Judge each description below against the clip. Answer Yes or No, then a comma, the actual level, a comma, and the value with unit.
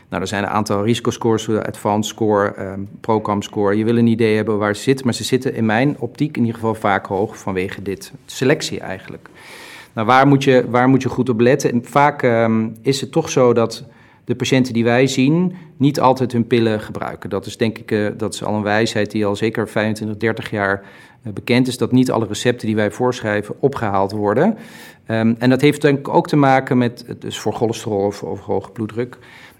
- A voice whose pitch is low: Yes, low, 115 Hz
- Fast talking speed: Yes, fast, 215 wpm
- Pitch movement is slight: No, average, 3.2 semitones